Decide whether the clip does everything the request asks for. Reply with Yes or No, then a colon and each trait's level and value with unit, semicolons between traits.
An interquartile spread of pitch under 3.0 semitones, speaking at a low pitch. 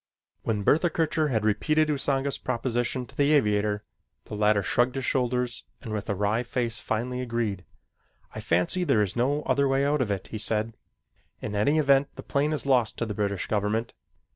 No: average, 4.6 semitones; low, 120 Hz